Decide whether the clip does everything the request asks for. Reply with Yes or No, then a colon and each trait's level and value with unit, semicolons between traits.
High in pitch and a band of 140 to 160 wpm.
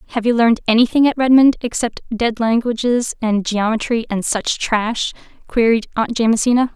Yes: high, 230 Hz; average, 150 wpm